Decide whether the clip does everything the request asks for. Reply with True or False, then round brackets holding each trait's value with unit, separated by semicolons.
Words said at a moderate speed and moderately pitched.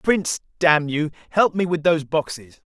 True (175 wpm; 160 Hz)